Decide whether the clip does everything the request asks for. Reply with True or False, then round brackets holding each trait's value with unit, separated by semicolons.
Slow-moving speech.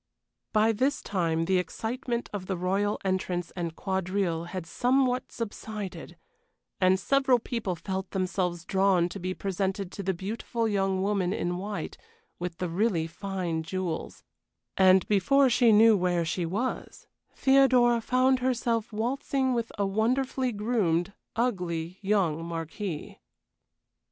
True (130 wpm)